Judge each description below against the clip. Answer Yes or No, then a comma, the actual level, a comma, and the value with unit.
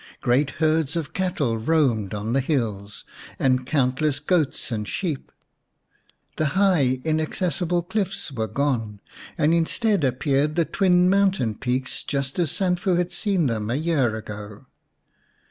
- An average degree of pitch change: No, wide, 5.9 semitones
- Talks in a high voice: No, medium, 145 Hz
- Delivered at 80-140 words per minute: Yes, slow, 135 wpm